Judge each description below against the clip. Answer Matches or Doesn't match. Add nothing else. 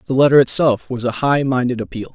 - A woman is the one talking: Doesn't match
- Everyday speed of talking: Doesn't match